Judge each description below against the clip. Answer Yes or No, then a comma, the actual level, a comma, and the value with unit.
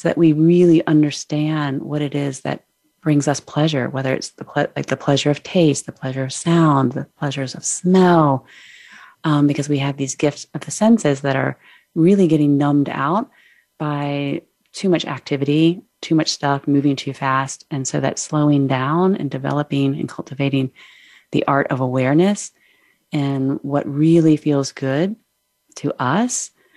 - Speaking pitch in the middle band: Yes, medium, 145 Hz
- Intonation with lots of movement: No, average, 2.8 semitones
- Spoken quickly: No, average, 165 wpm